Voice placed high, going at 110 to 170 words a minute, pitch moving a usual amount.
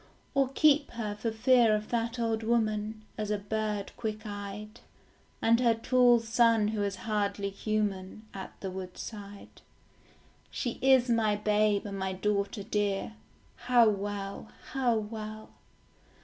No: high, 215 Hz; slow, 135 wpm; narrow, 2.1 semitones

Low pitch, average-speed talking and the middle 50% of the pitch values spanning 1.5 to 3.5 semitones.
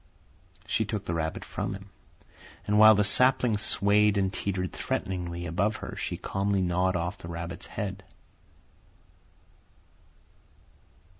No: very low, 95 Hz; slow, 125 wpm; average, 2.8 semitones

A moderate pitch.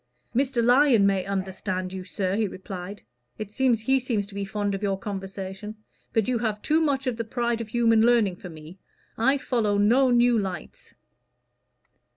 No: high, 215 Hz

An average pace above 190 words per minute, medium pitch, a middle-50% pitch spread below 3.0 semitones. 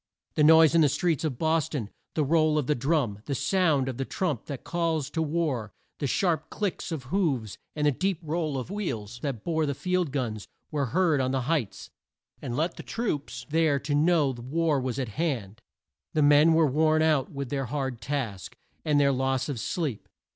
No: average, 200 wpm; medium, 145 Hz; average, 3.7 semitones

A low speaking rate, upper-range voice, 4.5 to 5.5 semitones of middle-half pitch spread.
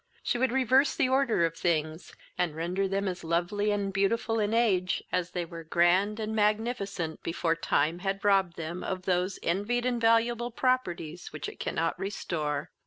No: average, 175 wpm; high, 195 Hz; average, 4.8 semitones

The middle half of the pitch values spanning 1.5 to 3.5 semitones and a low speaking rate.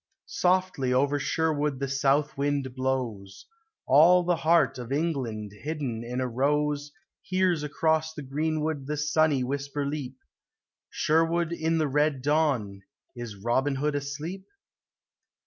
Yes: average, 3.2 semitones; slow, 130 wpm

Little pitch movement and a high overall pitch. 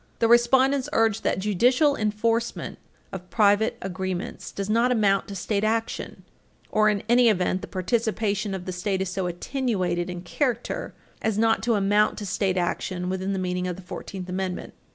No: average, 3.5 semitones; high, 205 Hz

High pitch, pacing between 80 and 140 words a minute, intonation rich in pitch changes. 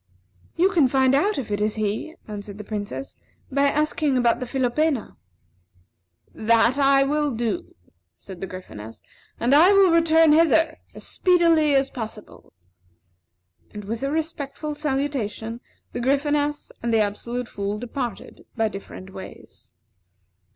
Yes: very high, 255 Hz; slow, 135 wpm; wide, 5.8 semitones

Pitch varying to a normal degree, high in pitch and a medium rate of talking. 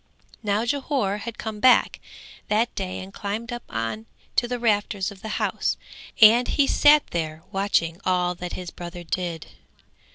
Yes: average, 4.8 semitones; high, 200 Hz; average, 160 wpm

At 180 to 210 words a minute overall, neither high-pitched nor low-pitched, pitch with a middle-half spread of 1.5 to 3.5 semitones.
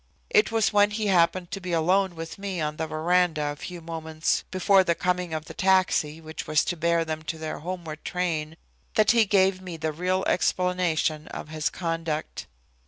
Yes: average, 190 wpm; medium, 170 Hz; average, 2.8 semitones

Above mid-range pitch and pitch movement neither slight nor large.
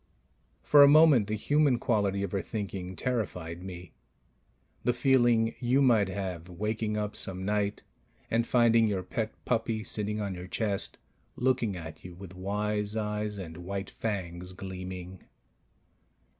No: low, 105 Hz; average, 3.4 semitones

